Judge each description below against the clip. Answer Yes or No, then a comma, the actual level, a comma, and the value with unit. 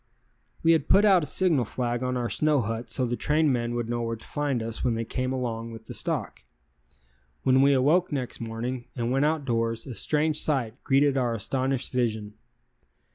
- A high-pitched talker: No, low, 125 Hz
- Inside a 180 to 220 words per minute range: Yes, average, 190 wpm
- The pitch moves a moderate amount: Yes, average, 3.7 semitones